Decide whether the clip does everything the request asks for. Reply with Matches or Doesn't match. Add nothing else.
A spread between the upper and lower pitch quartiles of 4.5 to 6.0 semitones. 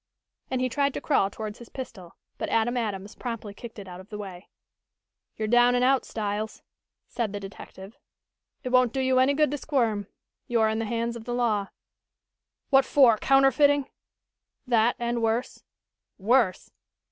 Doesn't match